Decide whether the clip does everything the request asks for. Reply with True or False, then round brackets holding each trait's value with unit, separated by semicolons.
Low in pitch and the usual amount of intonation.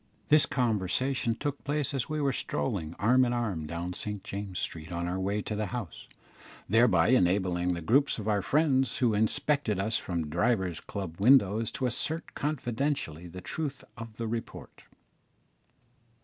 False (110 Hz; 6.0 semitones)